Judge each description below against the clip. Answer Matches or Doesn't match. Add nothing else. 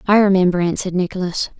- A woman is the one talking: Matches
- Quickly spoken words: Doesn't match